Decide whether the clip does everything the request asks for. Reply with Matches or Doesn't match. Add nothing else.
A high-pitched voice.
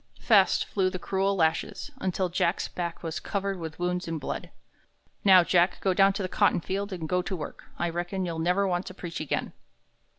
Doesn't match